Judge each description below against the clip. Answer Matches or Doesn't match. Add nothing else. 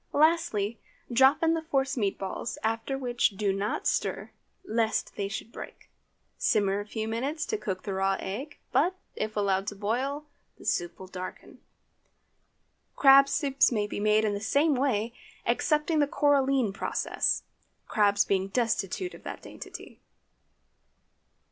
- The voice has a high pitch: Matches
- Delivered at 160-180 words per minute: Doesn't match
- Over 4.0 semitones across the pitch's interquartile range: Matches